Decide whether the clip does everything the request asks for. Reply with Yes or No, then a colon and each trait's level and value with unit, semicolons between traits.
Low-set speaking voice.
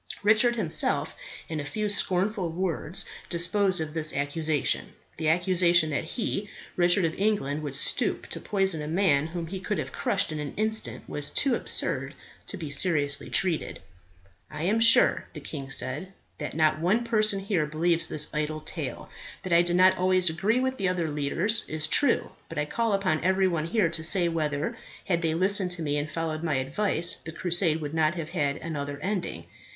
No: medium, 170 Hz